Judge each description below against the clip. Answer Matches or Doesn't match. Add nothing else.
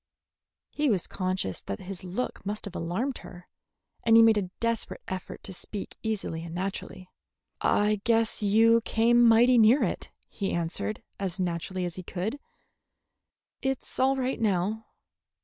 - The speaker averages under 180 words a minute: Matches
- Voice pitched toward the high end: Matches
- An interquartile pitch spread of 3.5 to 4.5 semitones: Matches